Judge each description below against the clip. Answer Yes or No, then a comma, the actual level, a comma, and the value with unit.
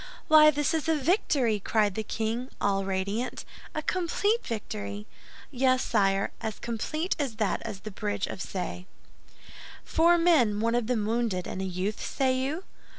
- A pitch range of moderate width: No, wide, 6.6 semitones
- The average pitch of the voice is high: Yes, high, 230 Hz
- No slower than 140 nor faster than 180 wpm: Yes, average, 160 wpm